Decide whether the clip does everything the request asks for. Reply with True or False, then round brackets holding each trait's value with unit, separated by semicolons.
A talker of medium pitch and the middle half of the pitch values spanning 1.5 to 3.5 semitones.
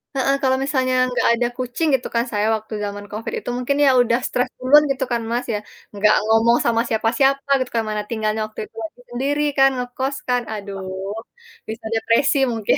False (235 Hz; 3.2 semitones)